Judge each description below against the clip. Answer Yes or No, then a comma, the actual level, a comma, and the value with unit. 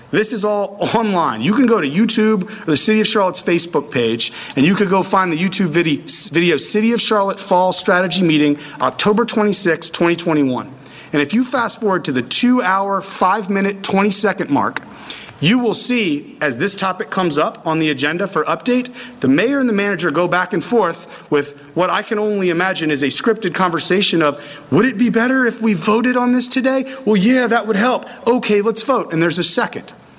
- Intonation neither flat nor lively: Yes, average, 5.0 semitones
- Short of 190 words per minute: No, average, 200 wpm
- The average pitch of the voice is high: Yes, high, 195 Hz